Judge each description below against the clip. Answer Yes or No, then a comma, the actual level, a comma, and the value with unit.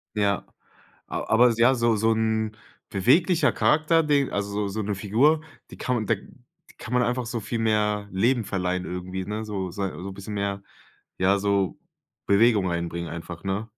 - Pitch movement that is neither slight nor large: Yes, average, 3.3 semitones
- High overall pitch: No, low, 105 Hz